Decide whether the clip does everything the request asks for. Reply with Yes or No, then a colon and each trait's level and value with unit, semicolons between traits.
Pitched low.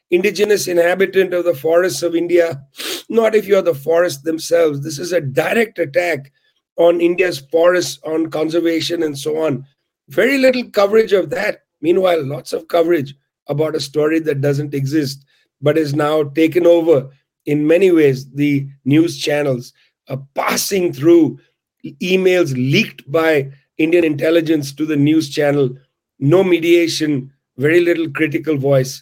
No: medium, 160 Hz